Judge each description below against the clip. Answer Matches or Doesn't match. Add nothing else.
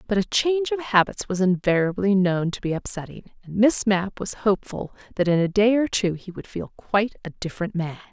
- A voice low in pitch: Doesn't match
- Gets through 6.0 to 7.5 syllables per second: Doesn't match